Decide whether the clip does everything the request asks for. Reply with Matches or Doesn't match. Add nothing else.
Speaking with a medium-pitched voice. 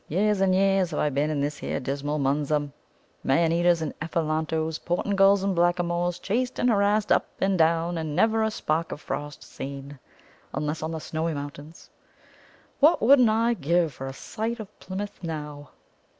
Matches